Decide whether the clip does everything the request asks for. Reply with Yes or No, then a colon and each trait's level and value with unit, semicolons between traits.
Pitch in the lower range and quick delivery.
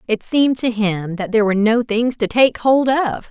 No: high, 230 Hz; fast, 235 wpm